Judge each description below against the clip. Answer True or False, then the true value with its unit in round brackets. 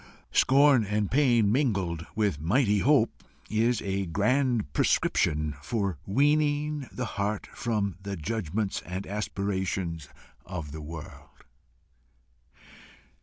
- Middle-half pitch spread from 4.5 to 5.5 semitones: True (5.2 semitones)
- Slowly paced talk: True (105 wpm)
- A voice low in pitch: True (100 Hz)